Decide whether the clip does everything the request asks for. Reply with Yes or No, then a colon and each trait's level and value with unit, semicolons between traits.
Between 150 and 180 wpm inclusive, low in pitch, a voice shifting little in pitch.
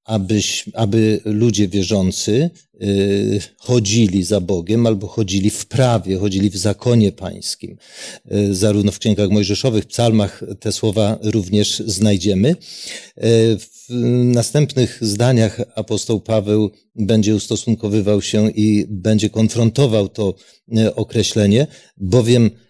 No: average, 115 wpm; low, 110 Hz; narrow, 1.7 semitones